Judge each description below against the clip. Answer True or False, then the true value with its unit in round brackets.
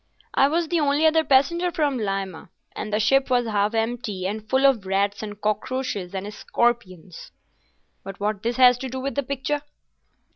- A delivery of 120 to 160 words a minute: False (180 wpm)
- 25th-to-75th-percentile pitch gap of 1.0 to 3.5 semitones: False (5.1 semitones)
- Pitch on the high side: True (235 Hz)